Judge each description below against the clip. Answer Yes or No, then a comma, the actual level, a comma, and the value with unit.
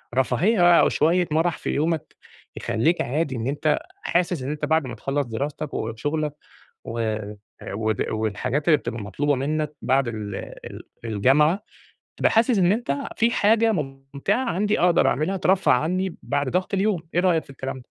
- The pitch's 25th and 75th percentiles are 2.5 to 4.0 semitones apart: No, wide, 5.4 semitones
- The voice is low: No, medium, 150 Hz